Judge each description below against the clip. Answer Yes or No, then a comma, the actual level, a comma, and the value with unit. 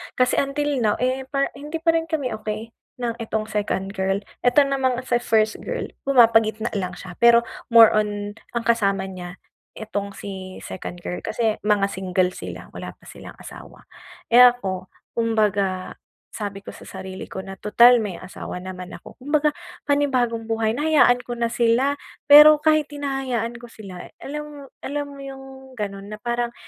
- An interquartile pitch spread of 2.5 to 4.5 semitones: No, average, 5.0 semitones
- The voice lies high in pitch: Yes, high, 230 Hz